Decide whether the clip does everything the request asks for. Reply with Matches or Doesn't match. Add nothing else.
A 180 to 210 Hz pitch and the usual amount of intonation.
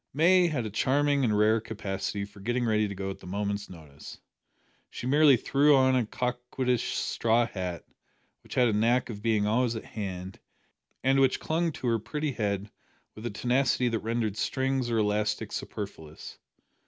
Doesn't match